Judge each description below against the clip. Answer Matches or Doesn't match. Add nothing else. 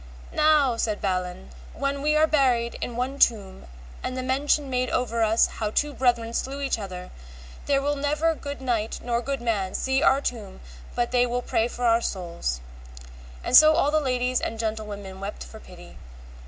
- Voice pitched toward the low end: Doesn't match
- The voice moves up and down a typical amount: Matches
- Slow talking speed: Doesn't match